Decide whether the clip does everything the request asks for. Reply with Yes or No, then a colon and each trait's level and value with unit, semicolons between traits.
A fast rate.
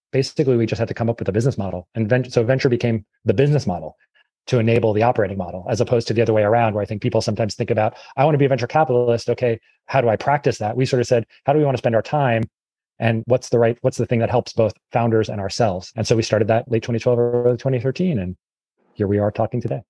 Yes: fast, 275 wpm